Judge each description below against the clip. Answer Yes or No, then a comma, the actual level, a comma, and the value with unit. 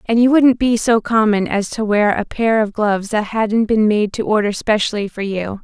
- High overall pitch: Yes, high, 215 Hz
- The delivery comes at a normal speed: No, fast, 235 wpm